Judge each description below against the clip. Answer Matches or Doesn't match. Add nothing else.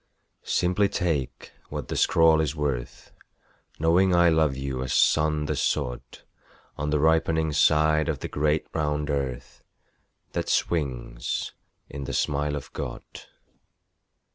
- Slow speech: Matches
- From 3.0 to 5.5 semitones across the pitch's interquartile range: Doesn't match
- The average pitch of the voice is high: Doesn't match